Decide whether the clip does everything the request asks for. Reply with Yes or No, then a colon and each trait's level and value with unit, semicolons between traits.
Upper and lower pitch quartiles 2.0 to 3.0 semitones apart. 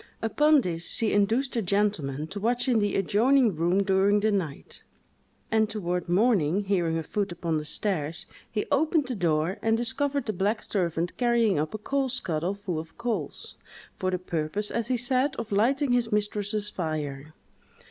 No: average, 5.3 semitones